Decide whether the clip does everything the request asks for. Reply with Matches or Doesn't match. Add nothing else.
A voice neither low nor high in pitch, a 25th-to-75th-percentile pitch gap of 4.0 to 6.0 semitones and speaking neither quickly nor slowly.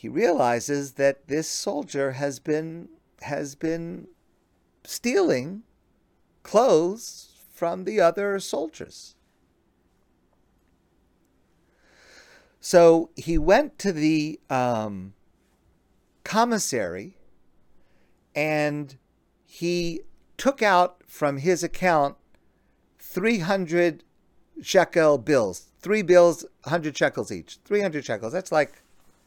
Doesn't match